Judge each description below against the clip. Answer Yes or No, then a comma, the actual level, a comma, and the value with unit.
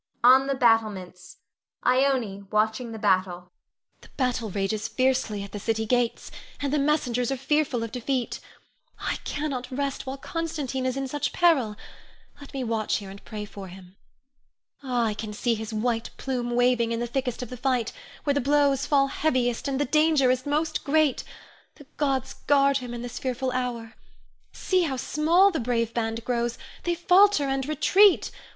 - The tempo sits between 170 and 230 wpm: Yes, average, 175 wpm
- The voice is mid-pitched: No, very high, 250 Hz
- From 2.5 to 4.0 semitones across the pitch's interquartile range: Yes, average, 3.6 semitones